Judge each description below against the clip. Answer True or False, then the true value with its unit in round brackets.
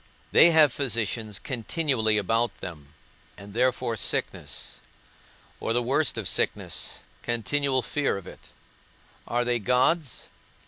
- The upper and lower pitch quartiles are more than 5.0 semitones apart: False (3.6 semitones)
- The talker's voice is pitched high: False (120 Hz)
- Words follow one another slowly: True (120 wpm)